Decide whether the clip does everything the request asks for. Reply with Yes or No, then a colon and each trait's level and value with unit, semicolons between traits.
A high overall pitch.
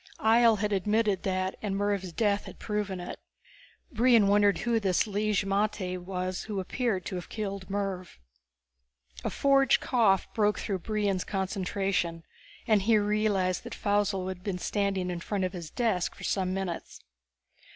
Yes: high, 200 Hz